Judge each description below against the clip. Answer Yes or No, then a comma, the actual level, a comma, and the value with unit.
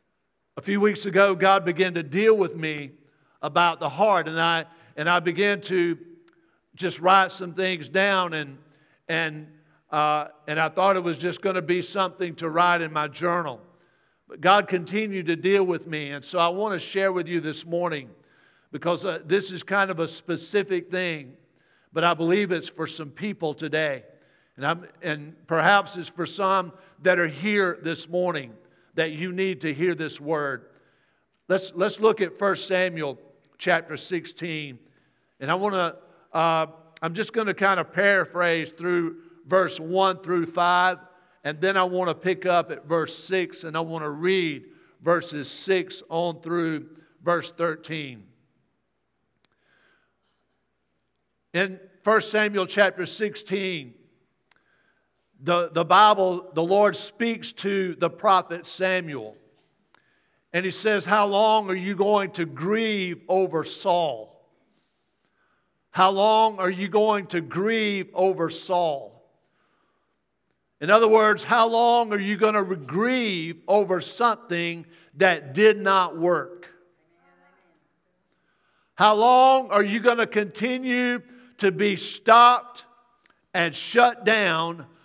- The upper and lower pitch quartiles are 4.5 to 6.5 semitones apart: No, average, 3.2 semitones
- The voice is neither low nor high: Yes, medium, 180 Hz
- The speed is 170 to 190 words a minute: No, average, 145 wpm